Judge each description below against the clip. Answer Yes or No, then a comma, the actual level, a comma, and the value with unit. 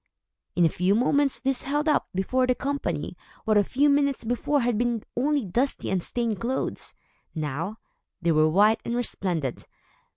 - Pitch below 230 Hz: No, high, 235 Hz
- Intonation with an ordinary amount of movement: No, wide, 6.4 semitones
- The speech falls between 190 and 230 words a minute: No, average, 165 wpm